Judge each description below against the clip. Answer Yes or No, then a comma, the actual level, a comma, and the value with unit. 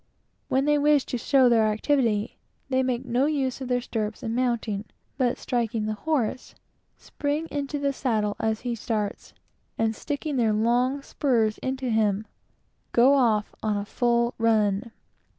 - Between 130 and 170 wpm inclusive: Yes, average, 155 wpm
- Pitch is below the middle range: No, high, 240 Hz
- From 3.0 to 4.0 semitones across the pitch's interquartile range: Yes, average, 3.5 semitones